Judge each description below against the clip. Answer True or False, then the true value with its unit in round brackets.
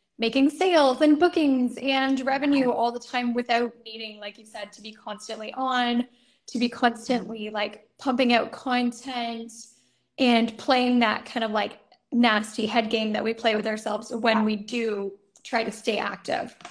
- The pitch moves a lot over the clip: False (2.4 semitones)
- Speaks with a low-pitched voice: False (235 Hz)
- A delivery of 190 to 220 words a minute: False (165 wpm)